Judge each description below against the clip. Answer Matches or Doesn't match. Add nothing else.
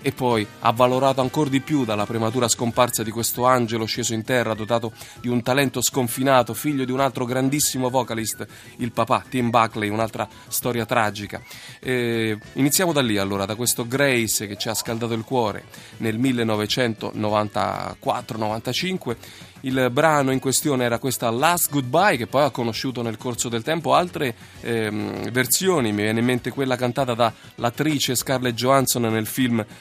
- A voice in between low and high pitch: Doesn't match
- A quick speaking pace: Doesn't match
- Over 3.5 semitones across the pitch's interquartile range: Doesn't match